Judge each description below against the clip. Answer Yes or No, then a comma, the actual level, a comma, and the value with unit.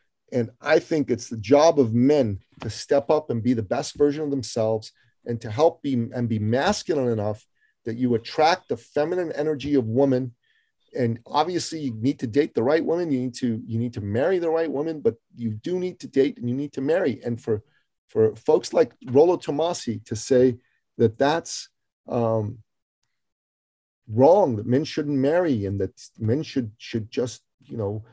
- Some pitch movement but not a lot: Yes, average, 4.3 semitones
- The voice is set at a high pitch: No, low, 125 Hz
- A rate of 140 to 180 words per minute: No, average, 190 wpm